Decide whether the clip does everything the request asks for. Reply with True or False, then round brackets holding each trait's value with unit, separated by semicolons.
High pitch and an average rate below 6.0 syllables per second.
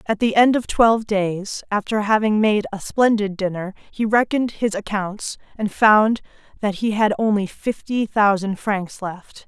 True (210 Hz; 4.3 syllables/s)